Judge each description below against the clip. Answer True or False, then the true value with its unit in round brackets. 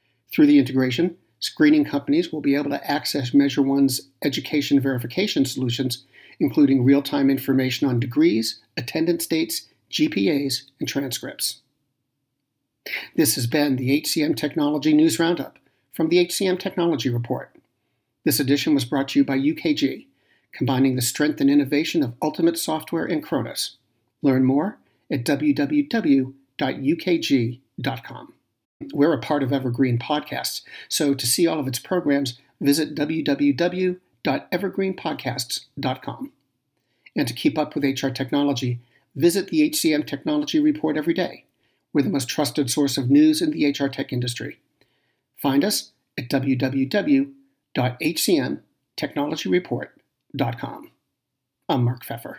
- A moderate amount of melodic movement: True (4.3 semitones)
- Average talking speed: False (125 wpm)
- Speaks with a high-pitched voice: False (145 Hz)